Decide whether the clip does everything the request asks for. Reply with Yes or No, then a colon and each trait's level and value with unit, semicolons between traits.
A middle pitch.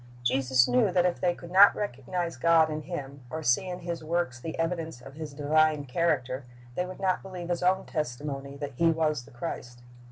Yes: medium, 155 Hz